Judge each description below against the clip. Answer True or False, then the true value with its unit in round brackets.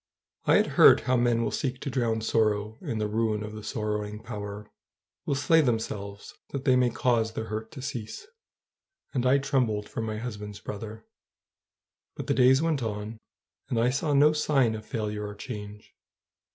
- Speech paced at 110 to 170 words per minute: False (180 wpm)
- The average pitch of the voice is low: True (110 Hz)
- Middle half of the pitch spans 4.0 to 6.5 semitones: False (3.2 semitones)